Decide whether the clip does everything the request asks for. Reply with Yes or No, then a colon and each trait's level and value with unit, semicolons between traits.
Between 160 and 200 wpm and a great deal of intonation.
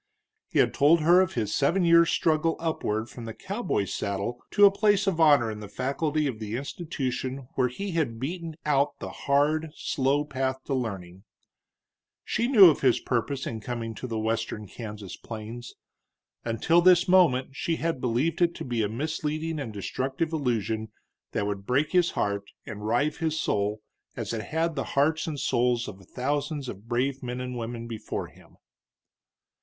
Yes: average, 175 wpm; wide, 5.9 semitones